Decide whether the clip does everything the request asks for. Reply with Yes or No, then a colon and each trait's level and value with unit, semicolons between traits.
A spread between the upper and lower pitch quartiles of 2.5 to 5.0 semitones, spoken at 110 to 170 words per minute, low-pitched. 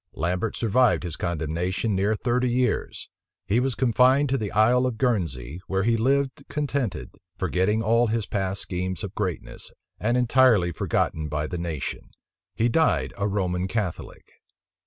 No: wide, 5.5 semitones; average, 150 wpm; low, 105 Hz